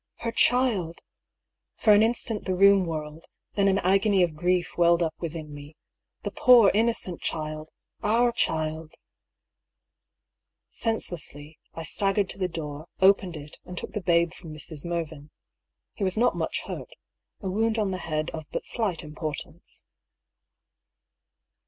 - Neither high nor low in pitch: Yes, medium, 175 Hz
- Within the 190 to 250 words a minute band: No, average, 155 wpm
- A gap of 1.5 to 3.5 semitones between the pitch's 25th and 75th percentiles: No, average, 4.4 semitones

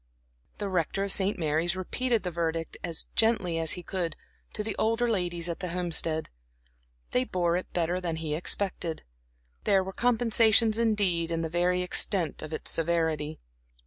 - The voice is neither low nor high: Yes, medium, 175 Hz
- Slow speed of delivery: No, average, 165 wpm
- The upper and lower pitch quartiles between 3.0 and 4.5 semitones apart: Yes, average, 3.3 semitones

